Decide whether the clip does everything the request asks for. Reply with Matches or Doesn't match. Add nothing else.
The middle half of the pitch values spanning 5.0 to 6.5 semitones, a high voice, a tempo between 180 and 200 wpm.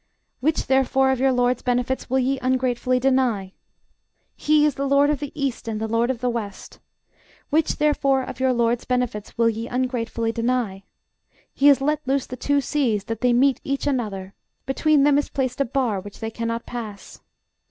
Doesn't match